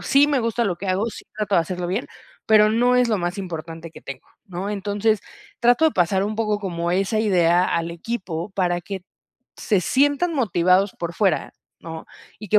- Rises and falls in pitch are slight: No, average, 4.0 semitones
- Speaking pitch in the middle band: No, high, 195 Hz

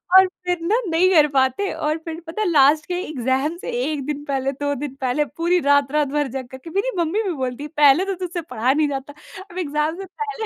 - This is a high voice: Yes, very high, 300 Hz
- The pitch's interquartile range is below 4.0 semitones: No, average, 4.3 semitones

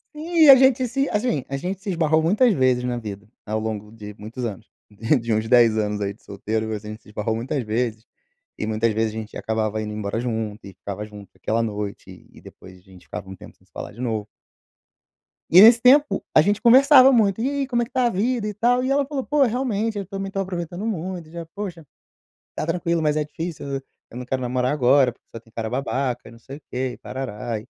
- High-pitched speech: No, low, 130 Hz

